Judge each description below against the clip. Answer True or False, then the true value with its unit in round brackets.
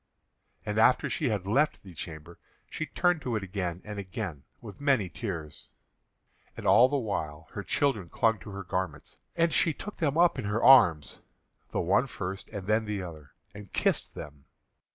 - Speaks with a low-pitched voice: True (100 Hz)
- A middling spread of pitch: False (6.5 semitones)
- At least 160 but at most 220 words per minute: True (180 wpm)